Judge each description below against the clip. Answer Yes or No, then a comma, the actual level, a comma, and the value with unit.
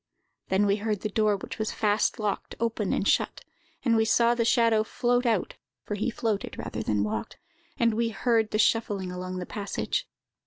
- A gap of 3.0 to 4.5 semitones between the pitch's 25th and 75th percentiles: No, narrow, 2.5 semitones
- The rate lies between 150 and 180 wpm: No, average, 190 wpm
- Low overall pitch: No, high, 215 Hz